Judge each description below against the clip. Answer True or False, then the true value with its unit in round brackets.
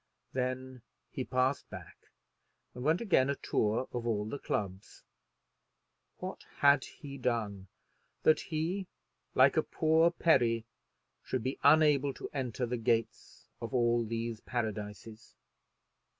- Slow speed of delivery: True (125 wpm)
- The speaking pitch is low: True (125 Hz)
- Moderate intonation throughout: True (3.7 semitones)